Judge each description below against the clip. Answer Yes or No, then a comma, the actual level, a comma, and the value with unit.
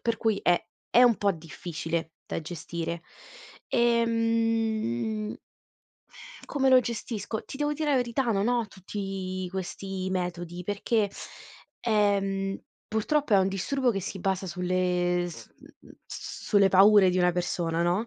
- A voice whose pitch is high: Yes, high, 195 Hz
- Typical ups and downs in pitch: Yes, average, 4.2 semitones